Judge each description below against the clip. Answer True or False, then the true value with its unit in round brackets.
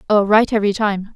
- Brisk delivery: True (210 wpm)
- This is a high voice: True (205 Hz)